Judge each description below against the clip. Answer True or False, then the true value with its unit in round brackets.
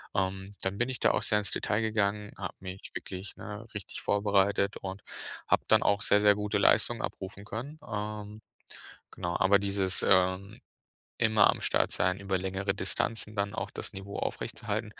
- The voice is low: True (100 Hz)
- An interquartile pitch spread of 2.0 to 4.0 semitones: False (1.5 semitones)